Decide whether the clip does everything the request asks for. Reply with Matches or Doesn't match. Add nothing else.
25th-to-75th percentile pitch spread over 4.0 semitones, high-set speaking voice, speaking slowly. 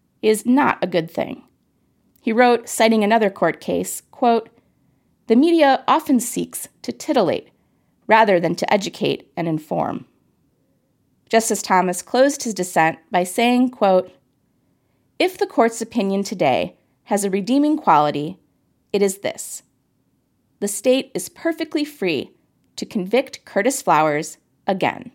Matches